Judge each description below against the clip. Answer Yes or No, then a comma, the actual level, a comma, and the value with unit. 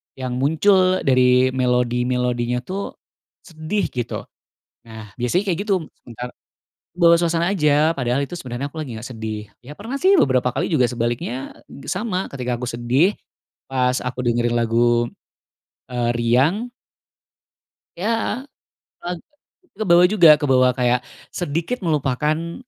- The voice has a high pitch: No, low, 130 Hz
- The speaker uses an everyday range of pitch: No, wide, 5.8 semitones